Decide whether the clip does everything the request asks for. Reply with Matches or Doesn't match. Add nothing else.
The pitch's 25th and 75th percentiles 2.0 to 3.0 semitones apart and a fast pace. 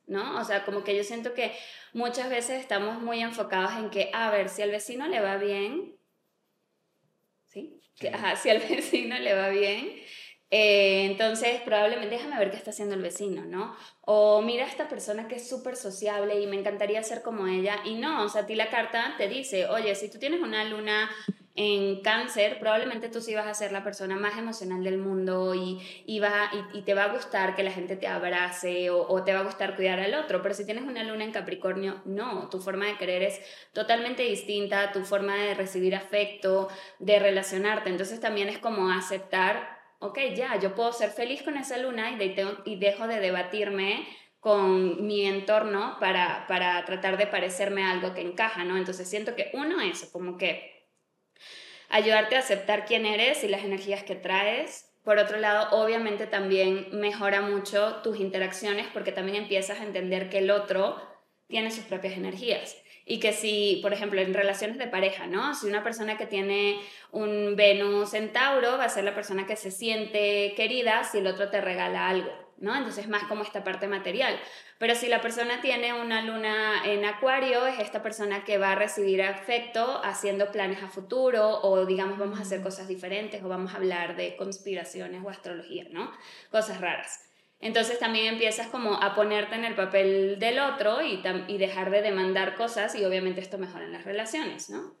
Matches